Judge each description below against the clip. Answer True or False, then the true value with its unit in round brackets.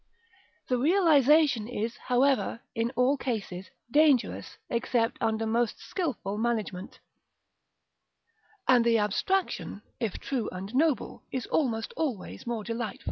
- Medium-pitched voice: False (235 Hz)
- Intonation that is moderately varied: True (3.6 semitones)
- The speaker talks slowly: True (115 wpm)